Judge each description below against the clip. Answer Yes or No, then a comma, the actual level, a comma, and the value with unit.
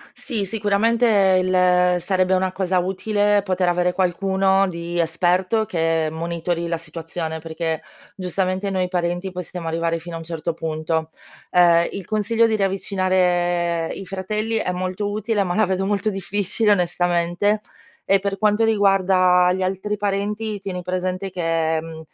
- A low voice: No, medium, 185 Hz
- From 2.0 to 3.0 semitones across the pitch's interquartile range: Yes, narrow, 2.5 semitones